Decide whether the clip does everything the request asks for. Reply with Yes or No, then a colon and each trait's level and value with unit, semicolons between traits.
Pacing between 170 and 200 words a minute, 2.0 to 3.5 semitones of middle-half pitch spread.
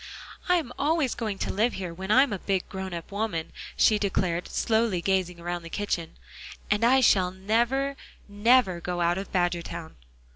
No: average, 175 wpm; average, 4.6 semitones